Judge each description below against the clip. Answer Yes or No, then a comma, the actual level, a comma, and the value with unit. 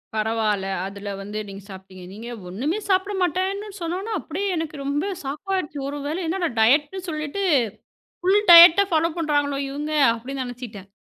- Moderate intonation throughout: No, wide, 8.0 semitones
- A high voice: Yes, very high, 295 Hz